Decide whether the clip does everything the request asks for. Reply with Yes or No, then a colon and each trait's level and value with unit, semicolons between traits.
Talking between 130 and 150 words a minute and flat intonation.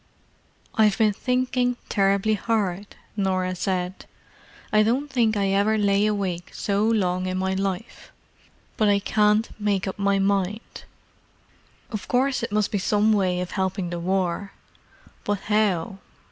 Yes: average, 145 wpm; narrow, 2.2 semitones